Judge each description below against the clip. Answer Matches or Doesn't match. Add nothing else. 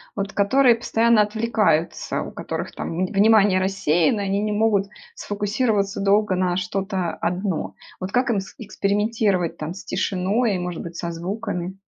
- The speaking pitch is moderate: Doesn't match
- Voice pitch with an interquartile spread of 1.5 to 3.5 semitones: Matches